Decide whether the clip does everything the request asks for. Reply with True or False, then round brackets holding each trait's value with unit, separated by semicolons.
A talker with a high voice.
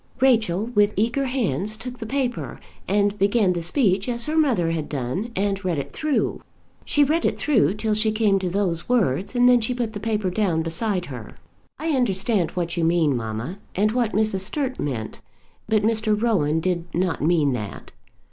True (205 Hz)